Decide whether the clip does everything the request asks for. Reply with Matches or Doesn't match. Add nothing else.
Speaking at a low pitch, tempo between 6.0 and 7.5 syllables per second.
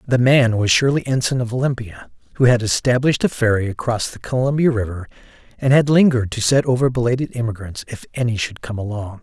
Matches